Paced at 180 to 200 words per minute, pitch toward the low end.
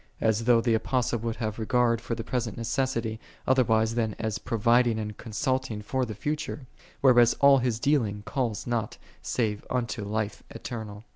No: average, 165 wpm; low, 115 Hz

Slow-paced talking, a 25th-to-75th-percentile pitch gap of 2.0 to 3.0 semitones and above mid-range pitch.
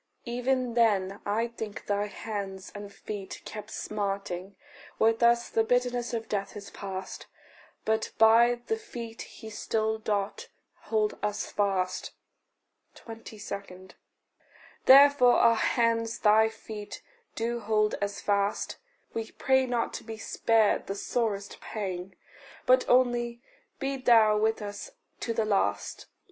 Yes: slow, 130 wpm; narrow, 2.6 semitones; high, 220 Hz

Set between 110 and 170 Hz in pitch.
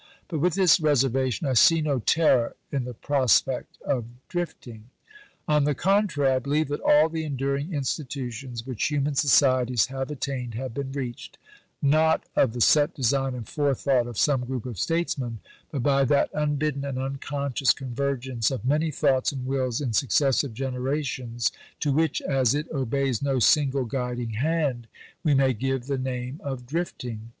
Yes: low, 135 Hz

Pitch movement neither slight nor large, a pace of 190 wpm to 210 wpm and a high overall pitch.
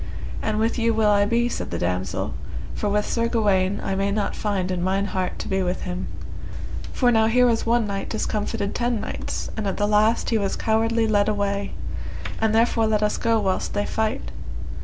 No: narrow, 2.2 semitones; fast, 205 wpm; high, 210 Hz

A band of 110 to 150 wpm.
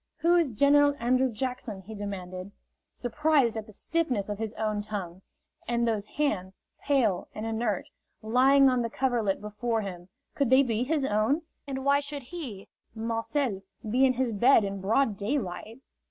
No: average, 165 wpm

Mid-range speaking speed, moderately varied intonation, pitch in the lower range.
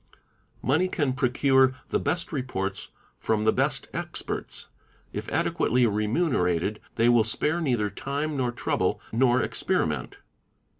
No: slow, 120 wpm; average, 4.4 semitones; low, 125 Hz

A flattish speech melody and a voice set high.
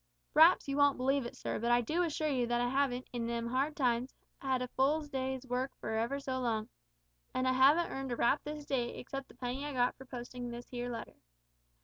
Yes: narrow, 2.3 semitones; very high, 255 Hz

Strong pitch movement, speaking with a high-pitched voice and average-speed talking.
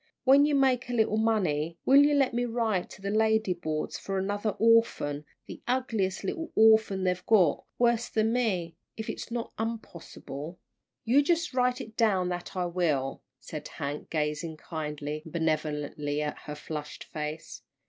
Yes: wide, 6.7 semitones; high, 195 Hz; average, 165 wpm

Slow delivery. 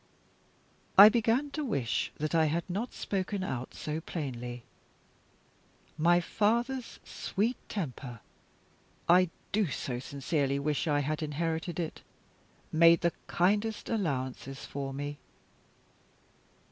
Yes: slow, 110 wpm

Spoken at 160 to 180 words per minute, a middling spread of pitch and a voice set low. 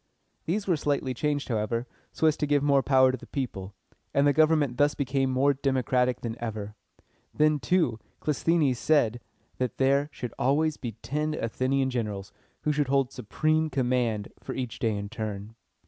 Yes: average, 175 wpm; average, 3.8 semitones; low, 130 Hz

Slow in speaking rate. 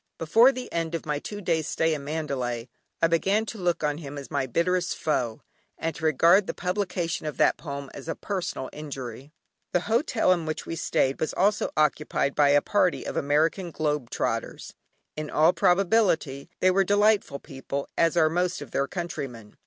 No: average, 185 wpm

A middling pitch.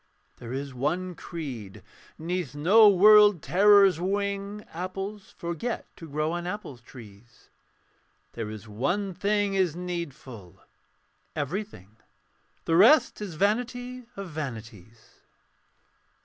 Yes: medium, 175 Hz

